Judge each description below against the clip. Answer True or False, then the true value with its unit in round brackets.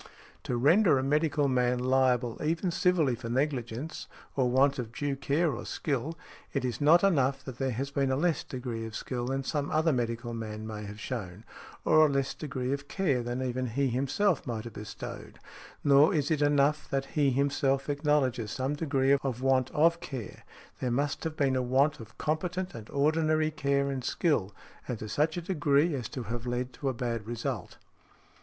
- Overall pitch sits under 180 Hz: True (135 Hz)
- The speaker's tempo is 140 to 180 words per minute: False (190 wpm)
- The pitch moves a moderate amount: True (3.3 semitones)